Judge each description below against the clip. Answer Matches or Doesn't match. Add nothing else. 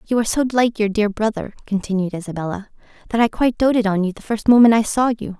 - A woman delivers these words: Matches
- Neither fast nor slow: Doesn't match